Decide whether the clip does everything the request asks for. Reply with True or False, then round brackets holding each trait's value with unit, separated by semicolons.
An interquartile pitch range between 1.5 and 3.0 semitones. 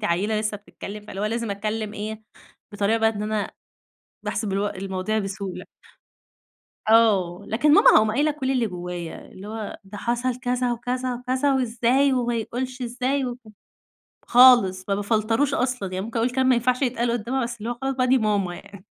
False (3.5 semitones)